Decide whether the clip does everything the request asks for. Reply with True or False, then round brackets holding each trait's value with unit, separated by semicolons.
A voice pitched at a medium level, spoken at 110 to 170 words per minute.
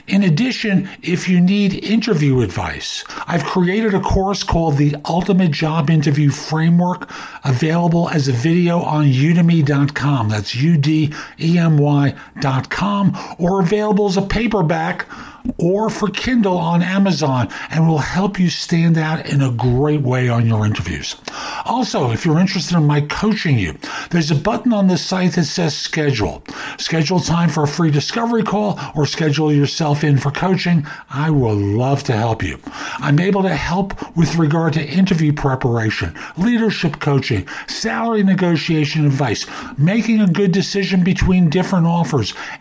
True (165 Hz; 155 wpm)